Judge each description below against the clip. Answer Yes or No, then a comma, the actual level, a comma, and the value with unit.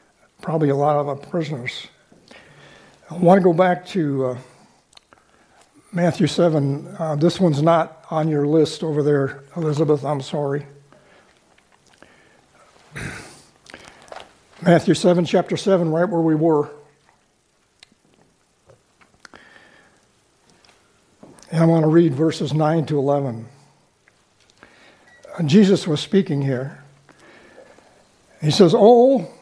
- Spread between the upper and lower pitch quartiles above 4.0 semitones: No, average, 3.0 semitones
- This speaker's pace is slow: Yes, slow, 100 wpm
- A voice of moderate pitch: Yes, medium, 160 Hz